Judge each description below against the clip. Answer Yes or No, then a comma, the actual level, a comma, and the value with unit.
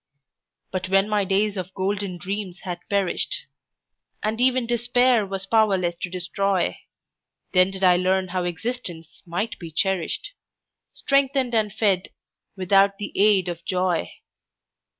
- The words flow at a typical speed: No, slow, 130 wpm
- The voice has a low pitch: No, high, 195 Hz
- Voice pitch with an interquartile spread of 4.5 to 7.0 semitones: No, average, 2.7 semitones